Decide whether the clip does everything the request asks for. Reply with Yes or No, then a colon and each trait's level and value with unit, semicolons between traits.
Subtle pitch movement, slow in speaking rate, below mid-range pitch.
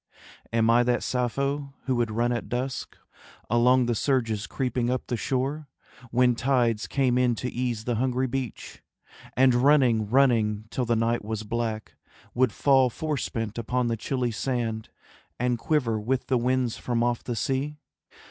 No: narrow, 2.0 semitones; average, 160 wpm; low, 125 Hz